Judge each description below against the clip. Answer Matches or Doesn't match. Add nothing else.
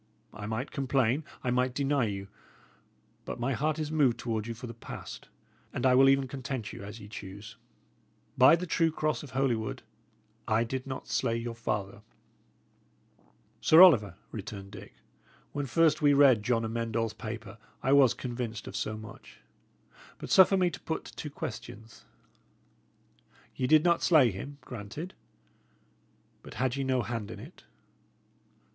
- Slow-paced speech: Doesn't match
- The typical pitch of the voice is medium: Doesn't match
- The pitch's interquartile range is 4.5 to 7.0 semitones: Doesn't match